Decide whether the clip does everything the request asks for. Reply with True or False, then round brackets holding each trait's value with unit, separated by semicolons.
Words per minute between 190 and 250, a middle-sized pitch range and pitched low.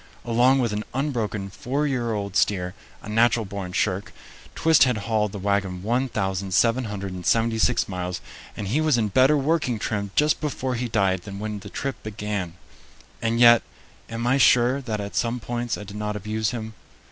False (170 wpm; 3.4 semitones; 110 Hz)